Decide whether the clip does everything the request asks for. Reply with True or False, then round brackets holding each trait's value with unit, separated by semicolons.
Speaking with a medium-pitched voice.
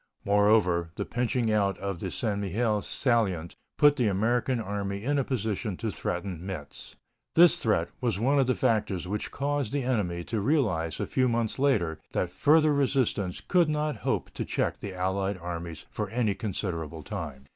False (105 Hz)